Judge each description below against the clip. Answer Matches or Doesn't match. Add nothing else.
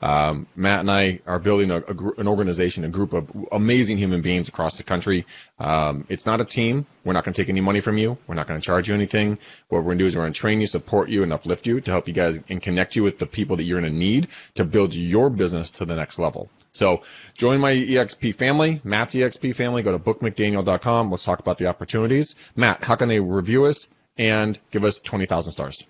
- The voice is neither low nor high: Doesn't match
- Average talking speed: Doesn't match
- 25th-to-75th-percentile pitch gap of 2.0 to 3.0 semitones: Doesn't match